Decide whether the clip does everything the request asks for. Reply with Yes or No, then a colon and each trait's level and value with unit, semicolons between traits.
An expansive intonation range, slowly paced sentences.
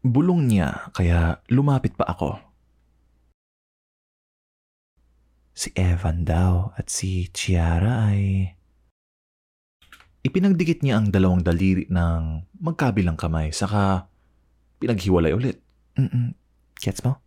Yes: wide, 8.0 semitones; slow, 95 wpm